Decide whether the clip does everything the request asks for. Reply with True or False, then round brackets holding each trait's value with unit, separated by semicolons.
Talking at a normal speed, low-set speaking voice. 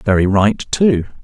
True (145 wpm; 110 Hz)